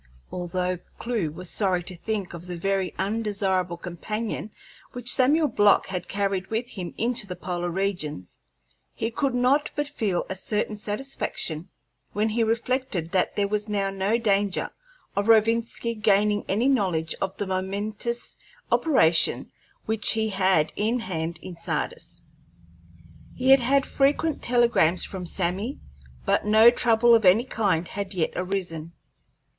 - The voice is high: Yes, high, 205 Hz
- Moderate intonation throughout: Yes, average, 4.1 semitones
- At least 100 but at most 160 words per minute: Yes, average, 145 wpm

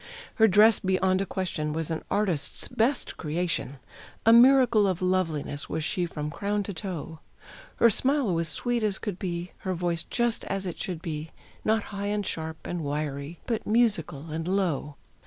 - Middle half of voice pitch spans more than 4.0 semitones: Yes, average, 4.6 semitones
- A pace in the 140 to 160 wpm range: No, average, 175 wpm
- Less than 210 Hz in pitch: Yes, medium, 185 Hz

